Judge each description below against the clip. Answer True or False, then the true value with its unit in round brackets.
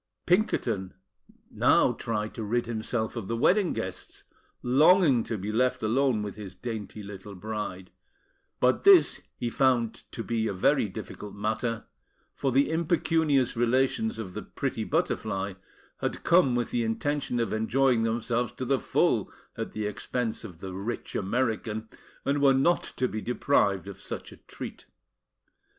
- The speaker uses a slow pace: False (155 wpm)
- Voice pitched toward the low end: True (115 Hz)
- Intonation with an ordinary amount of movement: True (3.9 semitones)